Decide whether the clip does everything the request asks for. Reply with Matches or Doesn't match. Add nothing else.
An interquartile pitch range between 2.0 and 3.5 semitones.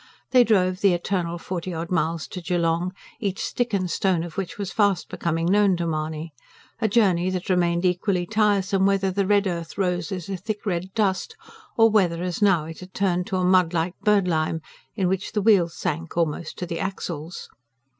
Matches